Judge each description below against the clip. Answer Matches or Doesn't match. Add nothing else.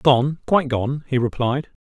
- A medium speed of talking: Matches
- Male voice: Matches